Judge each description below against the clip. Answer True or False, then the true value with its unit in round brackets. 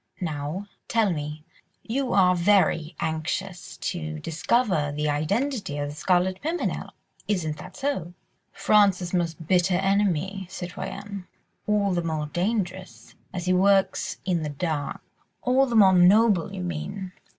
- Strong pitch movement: False (3.9 semitones)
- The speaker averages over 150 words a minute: False (135 wpm)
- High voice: False (180 Hz)